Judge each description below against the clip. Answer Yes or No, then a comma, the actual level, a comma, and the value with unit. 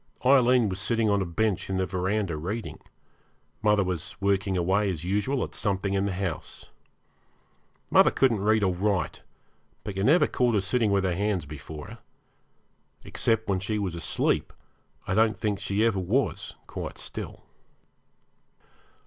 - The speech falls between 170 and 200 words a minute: No, average, 155 wpm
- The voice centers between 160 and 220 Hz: No, low, 100 Hz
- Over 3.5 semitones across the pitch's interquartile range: No, average, 2.7 semitones